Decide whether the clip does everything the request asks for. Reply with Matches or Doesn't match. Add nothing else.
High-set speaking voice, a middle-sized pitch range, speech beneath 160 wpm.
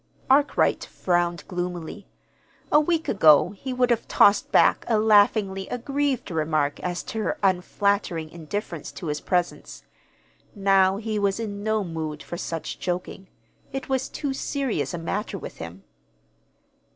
Matches